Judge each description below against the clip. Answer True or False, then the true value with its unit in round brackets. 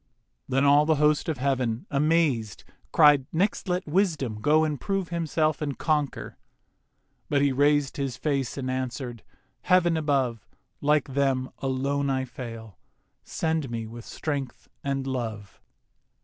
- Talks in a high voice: False (140 Hz)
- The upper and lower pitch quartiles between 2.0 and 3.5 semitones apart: True (3.0 semitones)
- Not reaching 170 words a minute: True (135 wpm)